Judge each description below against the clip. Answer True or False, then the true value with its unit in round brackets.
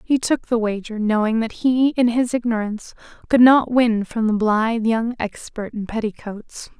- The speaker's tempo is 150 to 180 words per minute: True (175 wpm)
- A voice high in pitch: True (230 Hz)